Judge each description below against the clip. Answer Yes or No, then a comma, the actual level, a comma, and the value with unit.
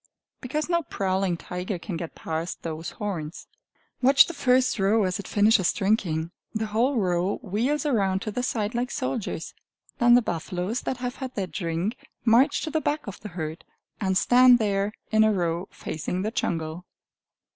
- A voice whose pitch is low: No, high, 205 Hz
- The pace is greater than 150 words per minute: Yes, average, 175 wpm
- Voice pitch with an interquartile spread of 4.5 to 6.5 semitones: Yes, wide, 5.5 semitones